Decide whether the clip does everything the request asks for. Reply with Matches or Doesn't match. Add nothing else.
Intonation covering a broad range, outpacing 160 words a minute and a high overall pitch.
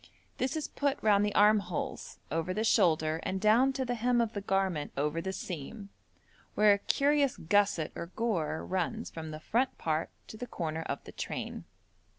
Matches